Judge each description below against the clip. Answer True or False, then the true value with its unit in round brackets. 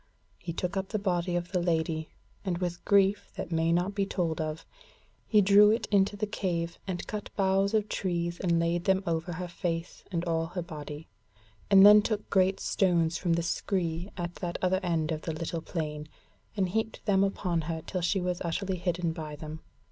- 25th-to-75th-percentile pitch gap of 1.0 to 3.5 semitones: True (2.7 semitones)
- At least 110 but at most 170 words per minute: False (200 wpm)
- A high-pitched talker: False (175 Hz)